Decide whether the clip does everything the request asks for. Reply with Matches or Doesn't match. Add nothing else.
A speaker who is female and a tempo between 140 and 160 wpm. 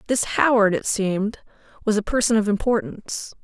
Matches